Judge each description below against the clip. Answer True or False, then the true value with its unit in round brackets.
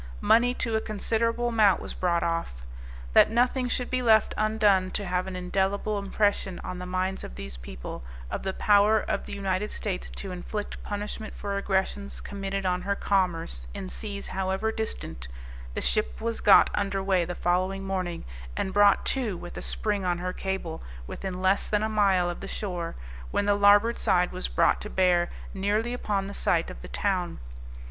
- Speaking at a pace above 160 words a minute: True (185 wpm)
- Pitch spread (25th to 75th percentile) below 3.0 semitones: True (2.5 semitones)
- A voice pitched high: True (195 Hz)